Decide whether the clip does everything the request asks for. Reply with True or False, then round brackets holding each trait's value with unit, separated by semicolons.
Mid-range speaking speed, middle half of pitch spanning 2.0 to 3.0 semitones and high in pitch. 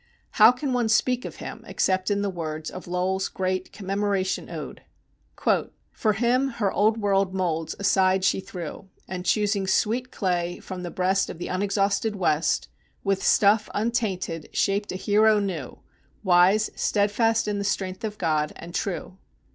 True (155 wpm; 2.4 semitones; 195 Hz)